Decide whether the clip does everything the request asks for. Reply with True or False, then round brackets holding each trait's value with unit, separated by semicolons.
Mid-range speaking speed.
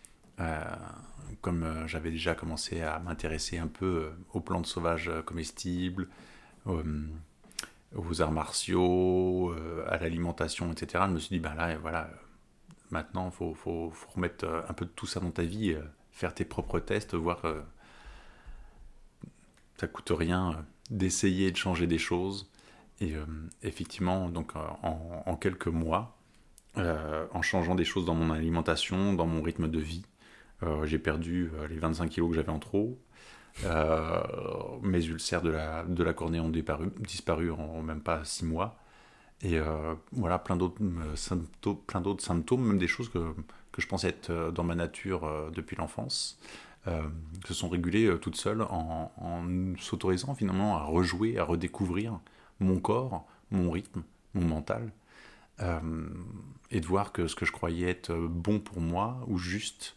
True (175 wpm)